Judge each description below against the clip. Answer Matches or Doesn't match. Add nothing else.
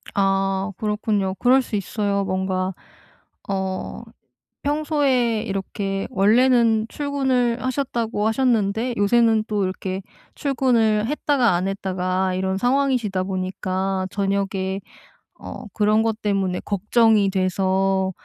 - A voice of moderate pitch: Doesn't match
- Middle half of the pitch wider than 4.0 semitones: Doesn't match